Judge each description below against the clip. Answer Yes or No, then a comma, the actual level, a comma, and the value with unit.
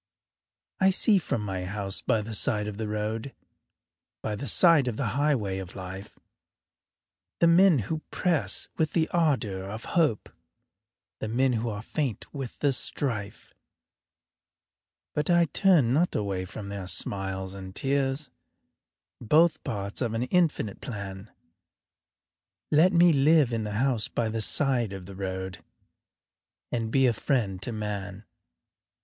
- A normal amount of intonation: No, wide, 6.3 semitones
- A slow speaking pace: No, average, 145 wpm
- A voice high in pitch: No, low, 115 Hz